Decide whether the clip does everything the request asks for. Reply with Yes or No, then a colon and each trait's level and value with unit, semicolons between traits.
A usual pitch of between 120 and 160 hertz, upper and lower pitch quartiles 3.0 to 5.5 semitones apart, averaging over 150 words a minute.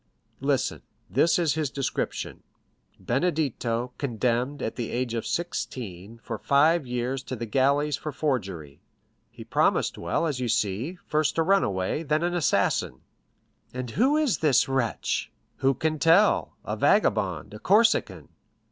No: low, 135 Hz; average, 5.1 semitones; slow, 135 wpm